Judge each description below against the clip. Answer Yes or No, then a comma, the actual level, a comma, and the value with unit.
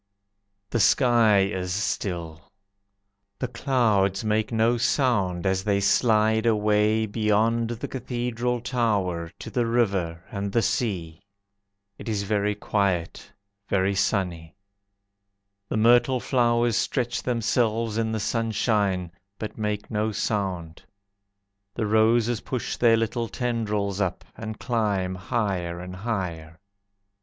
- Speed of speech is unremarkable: No, slow, 115 wpm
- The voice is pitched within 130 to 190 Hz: No, low, 105 Hz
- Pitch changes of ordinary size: Yes, average, 3.3 semitones